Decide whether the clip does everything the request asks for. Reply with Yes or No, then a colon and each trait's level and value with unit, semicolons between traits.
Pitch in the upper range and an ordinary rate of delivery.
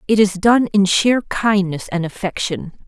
Yes: high, 195 Hz; average, 165 wpm